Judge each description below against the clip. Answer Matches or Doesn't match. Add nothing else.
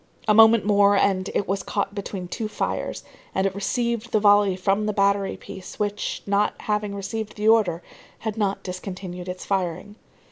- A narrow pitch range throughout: Matches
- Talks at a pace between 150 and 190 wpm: Matches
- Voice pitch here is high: Matches